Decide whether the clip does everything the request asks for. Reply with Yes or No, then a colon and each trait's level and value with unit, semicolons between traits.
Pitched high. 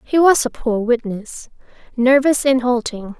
Yes: very high, 250 Hz